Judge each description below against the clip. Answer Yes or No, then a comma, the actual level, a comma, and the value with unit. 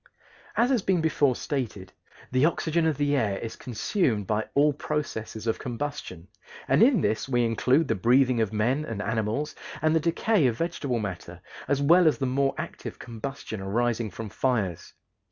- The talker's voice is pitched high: No, low, 125 Hz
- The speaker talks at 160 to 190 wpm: Yes, average, 170 wpm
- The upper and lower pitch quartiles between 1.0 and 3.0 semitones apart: No, average, 5.3 semitones